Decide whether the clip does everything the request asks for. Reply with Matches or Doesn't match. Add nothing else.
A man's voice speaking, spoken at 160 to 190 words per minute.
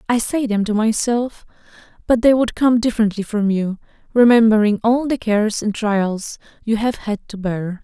Doesn't match